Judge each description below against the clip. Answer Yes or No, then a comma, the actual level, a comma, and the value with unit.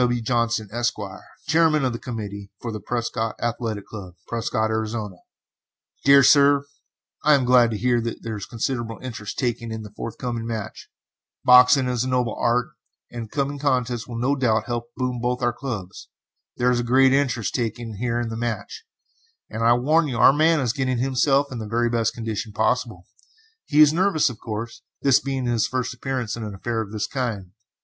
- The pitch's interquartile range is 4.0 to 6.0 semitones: No, narrow, 2.4 semitones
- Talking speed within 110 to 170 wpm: No, average, 195 wpm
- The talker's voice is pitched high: No, low, 120 Hz